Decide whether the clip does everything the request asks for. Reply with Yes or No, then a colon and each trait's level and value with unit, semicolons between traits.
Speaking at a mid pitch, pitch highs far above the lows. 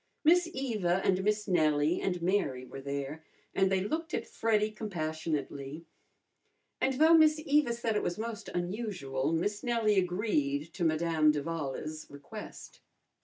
Yes: medium, 180 Hz; wide, 6.1 semitones